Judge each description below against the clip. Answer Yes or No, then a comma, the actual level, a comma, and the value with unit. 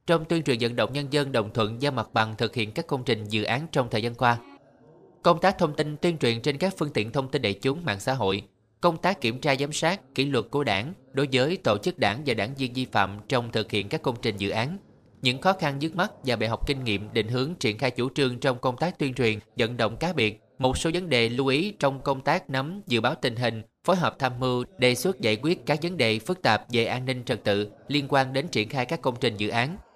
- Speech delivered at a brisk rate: Yes, fast, 270 wpm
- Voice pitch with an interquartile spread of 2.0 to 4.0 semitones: No, average, 4.7 semitones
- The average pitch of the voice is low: Yes, low, 130 Hz